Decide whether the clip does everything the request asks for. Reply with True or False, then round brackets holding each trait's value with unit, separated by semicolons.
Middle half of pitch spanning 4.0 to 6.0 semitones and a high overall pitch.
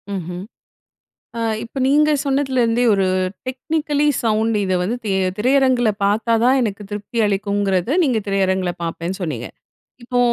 True (4.9 semitones; 220 Hz)